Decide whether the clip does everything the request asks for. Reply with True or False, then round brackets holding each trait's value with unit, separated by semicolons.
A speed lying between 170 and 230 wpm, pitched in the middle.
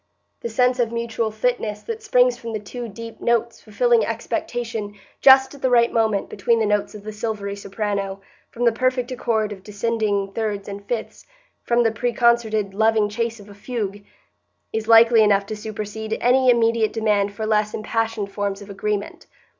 False (175 wpm; 220 Hz)